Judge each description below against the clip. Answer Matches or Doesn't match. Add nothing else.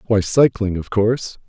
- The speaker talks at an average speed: Matches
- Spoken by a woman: Doesn't match